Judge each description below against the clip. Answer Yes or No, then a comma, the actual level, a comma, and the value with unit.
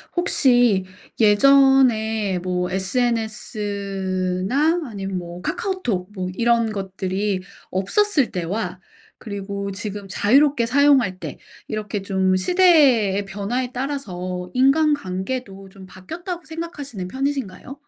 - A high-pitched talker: Yes, high, 210 Hz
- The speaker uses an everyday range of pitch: No, wide, 6.1 semitones